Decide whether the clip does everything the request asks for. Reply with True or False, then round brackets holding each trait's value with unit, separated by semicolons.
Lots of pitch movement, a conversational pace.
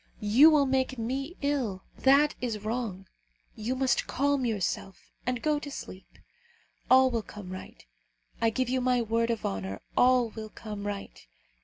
False (3.9 semitones; 160 wpm)